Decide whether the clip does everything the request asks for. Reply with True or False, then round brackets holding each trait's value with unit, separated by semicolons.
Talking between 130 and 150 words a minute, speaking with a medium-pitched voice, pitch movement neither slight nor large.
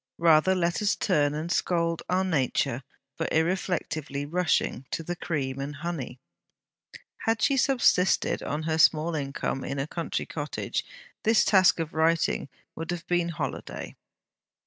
True (145 wpm; 165 Hz; 3.1 semitones)